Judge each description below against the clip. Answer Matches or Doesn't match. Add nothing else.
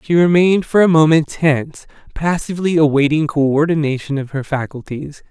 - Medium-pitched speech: Matches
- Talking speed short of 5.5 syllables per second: Doesn't match